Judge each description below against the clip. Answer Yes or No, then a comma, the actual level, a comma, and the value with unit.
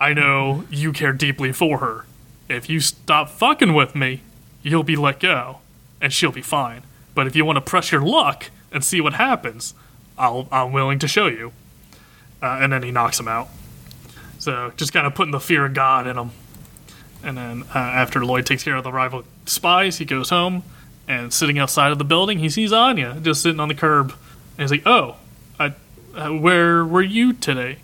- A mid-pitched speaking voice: Yes, medium, 145 Hz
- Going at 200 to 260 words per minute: Yes, fast, 205 wpm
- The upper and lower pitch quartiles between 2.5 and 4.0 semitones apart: Yes, average, 3.6 semitones